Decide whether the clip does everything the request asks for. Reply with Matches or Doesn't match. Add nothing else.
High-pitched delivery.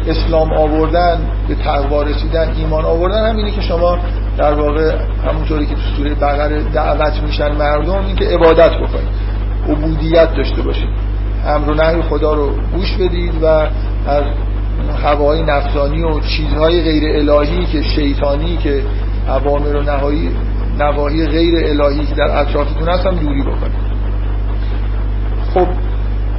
Doesn't match